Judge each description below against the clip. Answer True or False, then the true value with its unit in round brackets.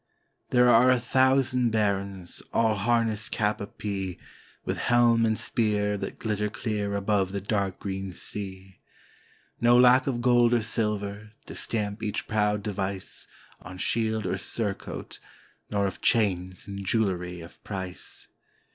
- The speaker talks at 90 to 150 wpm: True (145 wpm)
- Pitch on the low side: True (105 Hz)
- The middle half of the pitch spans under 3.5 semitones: True (2.8 semitones)